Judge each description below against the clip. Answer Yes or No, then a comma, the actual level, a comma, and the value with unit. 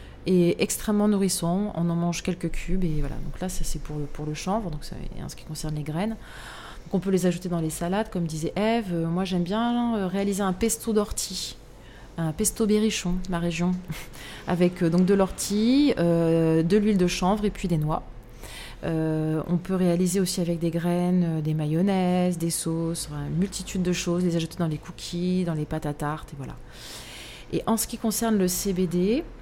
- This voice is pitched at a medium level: Yes, medium, 175 Hz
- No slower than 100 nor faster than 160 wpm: No, average, 210 wpm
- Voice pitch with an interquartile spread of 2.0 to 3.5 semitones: Yes, average, 3.1 semitones